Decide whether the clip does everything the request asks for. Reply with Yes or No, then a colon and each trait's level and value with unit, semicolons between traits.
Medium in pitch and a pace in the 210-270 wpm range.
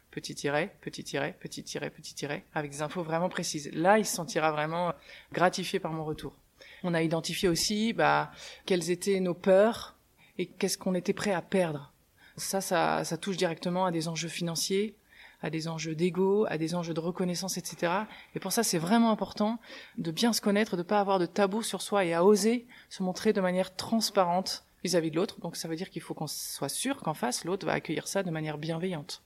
Yes: medium, 180 Hz; average, 215 wpm